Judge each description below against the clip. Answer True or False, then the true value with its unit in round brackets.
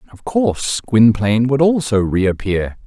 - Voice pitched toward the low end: True (120 Hz)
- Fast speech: False (125 wpm)